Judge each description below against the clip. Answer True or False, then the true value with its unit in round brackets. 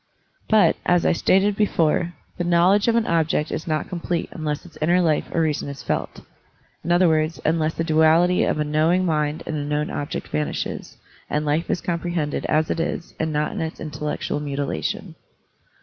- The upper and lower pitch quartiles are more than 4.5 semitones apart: False (2.4 semitones)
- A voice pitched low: False (160 Hz)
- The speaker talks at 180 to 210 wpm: True (190 wpm)